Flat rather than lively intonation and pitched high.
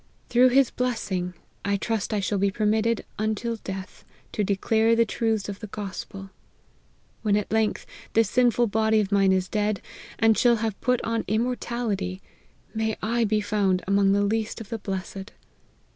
Yes: narrow, 2.3 semitones; high, 215 Hz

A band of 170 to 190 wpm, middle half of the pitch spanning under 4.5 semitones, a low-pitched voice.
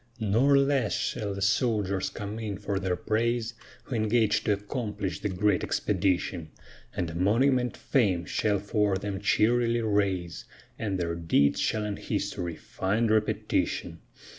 No: average, 140 wpm; average, 2.9 semitones; low, 105 Hz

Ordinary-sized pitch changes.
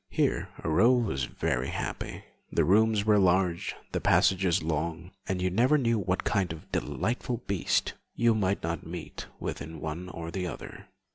Yes: average, 4.2 semitones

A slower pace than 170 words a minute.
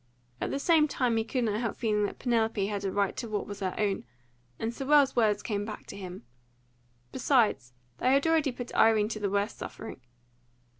No: average, 200 wpm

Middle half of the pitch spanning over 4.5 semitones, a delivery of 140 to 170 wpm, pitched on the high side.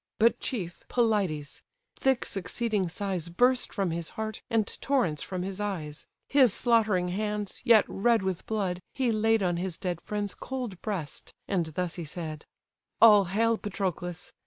No: average, 4.0 semitones; average, 155 wpm; high, 195 Hz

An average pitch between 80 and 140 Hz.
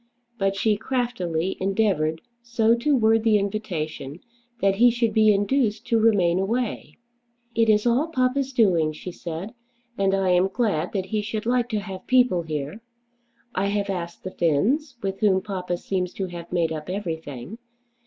No: high, 200 Hz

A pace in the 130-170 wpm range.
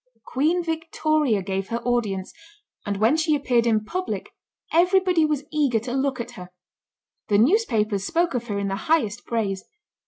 Yes: average, 160 wpm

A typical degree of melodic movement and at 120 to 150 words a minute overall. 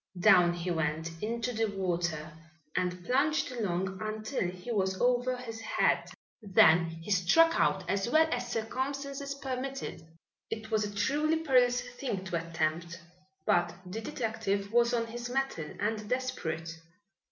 No: wide, 5.9 semitones; average, 140 wpm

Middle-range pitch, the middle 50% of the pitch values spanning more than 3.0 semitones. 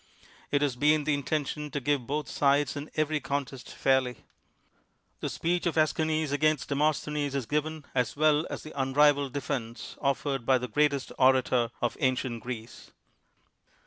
No: medium, 145 Hz; narrow, 2.4 semitones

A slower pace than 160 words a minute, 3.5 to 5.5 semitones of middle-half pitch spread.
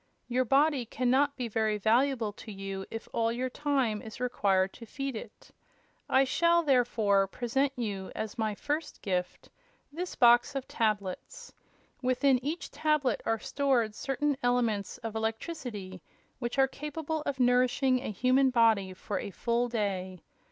Yes: average, 150 wpm; average, 4.1 semitones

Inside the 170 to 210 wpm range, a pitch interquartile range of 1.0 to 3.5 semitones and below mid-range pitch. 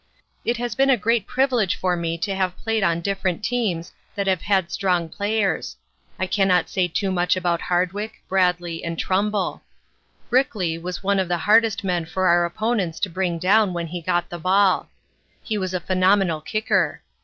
No: average, 180 wpm; average, 2.9 semitones; medium, 185 Hz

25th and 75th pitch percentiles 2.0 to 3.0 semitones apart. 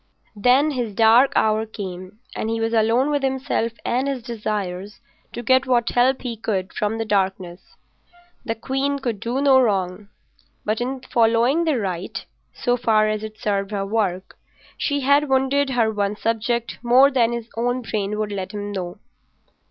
No: average, 3.7 semitones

